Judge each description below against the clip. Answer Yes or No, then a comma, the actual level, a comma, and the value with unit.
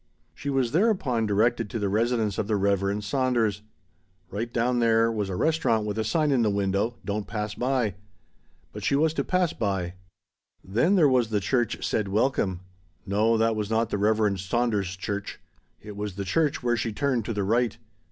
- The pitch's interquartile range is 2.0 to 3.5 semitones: Yes, average, 3.2 semitones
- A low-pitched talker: Yes, low, 110 Hz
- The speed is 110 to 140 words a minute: No, average, 190 wpm